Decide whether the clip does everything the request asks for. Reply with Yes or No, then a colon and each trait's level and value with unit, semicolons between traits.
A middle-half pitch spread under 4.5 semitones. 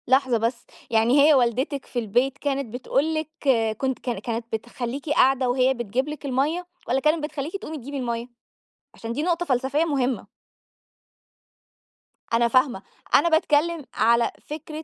Yes: average, 3.8 semitones